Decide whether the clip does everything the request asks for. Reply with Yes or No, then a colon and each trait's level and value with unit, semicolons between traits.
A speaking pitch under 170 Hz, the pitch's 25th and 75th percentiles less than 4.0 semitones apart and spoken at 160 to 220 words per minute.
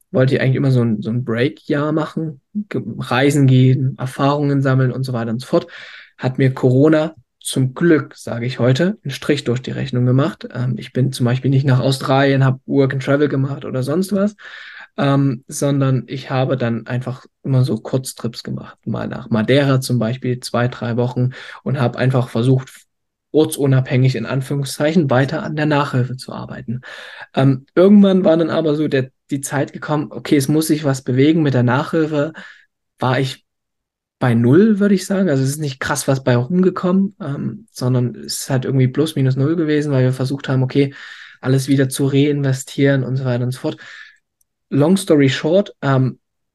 Yes: low, 135 Hz; average, 2.8 semitones; average, 185 wpm